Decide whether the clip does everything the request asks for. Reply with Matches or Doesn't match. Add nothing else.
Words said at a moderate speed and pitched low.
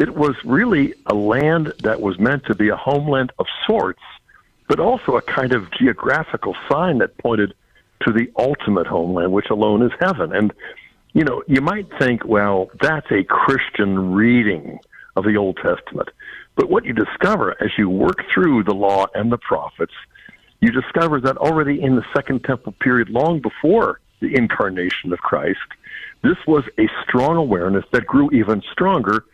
Matches